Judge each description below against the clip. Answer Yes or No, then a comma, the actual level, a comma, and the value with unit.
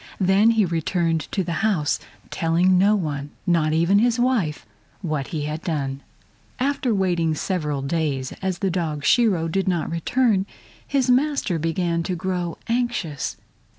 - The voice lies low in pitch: No, medium, 175 Hz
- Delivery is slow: No, average, 150 wpm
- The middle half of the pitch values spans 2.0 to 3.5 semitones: No, average, 4.2 semitones